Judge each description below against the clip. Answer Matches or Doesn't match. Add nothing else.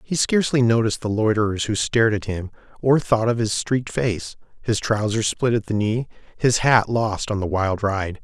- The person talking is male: Matches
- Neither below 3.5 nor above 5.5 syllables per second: Matches